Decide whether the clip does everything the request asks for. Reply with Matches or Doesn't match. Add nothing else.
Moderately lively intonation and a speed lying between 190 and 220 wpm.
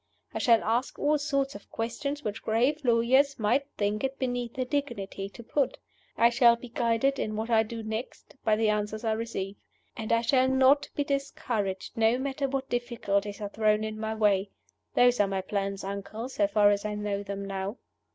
Matches